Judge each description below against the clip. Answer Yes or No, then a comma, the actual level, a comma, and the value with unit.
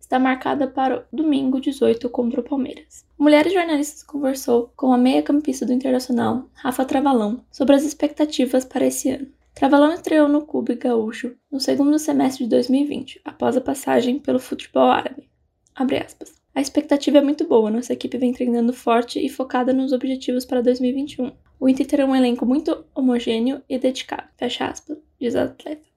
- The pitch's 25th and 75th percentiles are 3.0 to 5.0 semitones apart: No, narrow, 2.6 semitones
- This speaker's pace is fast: No, average, 170 wpm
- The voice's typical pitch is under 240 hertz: No, very high, 265 Hz